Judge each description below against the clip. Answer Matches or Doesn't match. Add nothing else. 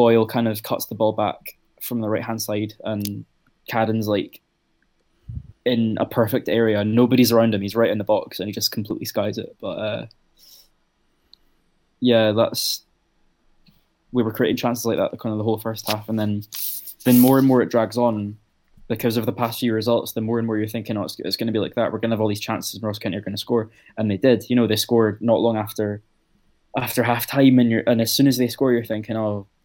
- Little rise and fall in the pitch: Matches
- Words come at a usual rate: Doesn't match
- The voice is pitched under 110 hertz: Doesn't match